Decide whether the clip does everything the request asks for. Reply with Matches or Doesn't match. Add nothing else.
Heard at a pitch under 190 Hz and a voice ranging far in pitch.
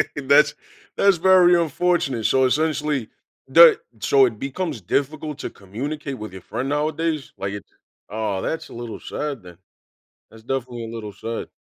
Matches